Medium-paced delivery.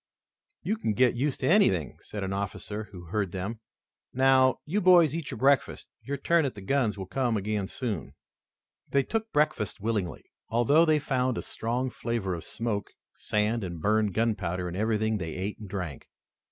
Yes: average, 180 wpm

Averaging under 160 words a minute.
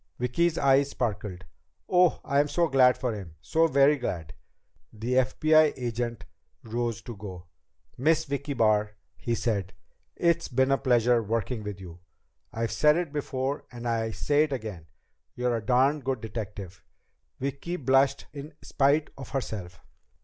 Yes: average, 150 wpm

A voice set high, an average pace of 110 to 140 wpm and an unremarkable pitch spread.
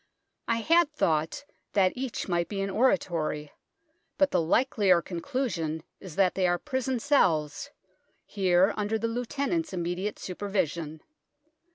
No: high, 195 Hz; slow, 135 wpm; wide, 6.6 semitones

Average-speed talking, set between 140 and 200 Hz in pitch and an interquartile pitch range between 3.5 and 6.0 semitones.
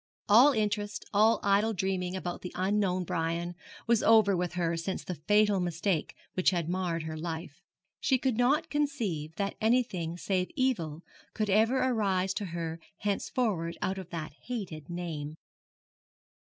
Yes: average, 150 wpm; high, 190 Hz; average, 4.2 semitones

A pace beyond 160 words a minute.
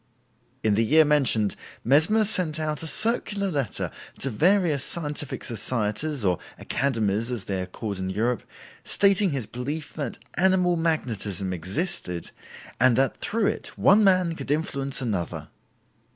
No: average, 140 wpm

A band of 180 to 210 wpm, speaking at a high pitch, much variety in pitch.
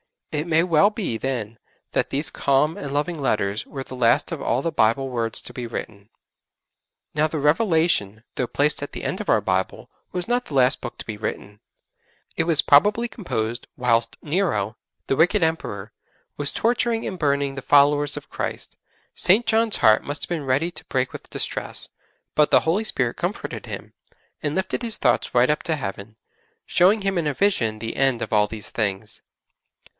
No: average, 190 wpm; medium, 140 Hz; wide, 6.3 semitones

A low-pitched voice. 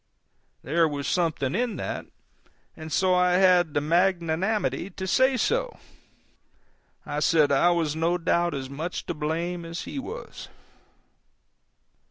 No: medium, 170 Hz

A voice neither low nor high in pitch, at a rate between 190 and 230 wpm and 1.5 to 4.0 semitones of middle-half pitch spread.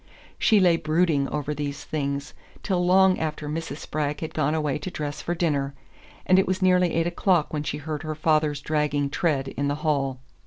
Yes: medium, 155 Hz; average, 195 wpm; average, 2.7 semitones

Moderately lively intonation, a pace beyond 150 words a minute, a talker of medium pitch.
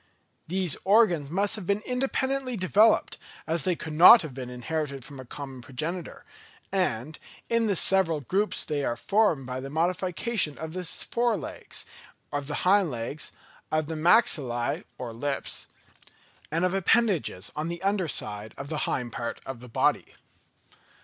No: wide, 6.0 semitones; average, 160 wpm; medium, 160 Hz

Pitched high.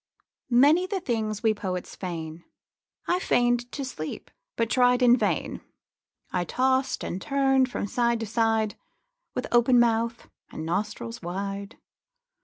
Yes: high, 230 Hz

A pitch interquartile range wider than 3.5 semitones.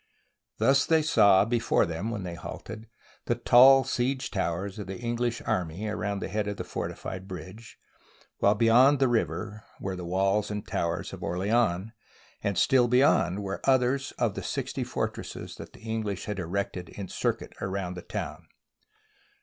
Yes: average, 4.1 semitones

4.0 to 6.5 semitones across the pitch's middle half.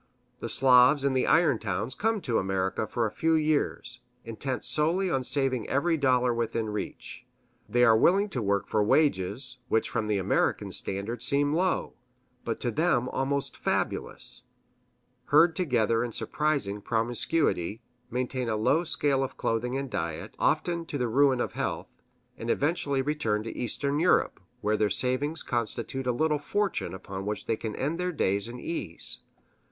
Yes: average, 4.9 semitones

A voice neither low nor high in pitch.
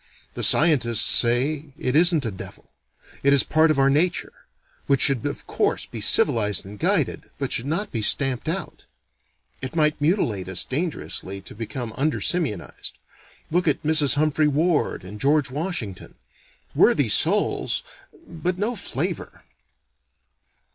Yes: medium, 145 Hz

